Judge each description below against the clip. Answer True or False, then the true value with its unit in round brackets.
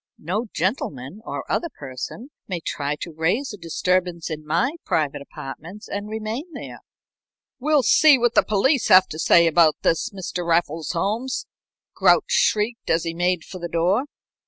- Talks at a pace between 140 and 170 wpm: True (160 wpm)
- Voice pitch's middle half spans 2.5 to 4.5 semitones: False (5.2 semitones)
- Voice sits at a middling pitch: True (180 Hz)